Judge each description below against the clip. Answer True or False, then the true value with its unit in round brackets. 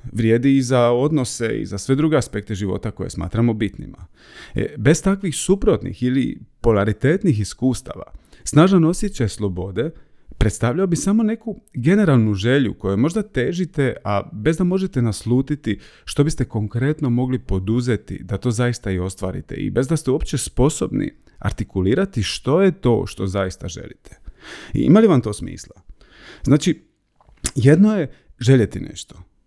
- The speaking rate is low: False (145 wpm)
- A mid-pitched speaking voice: False (125 Hz)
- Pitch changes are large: True (6.4 semitones)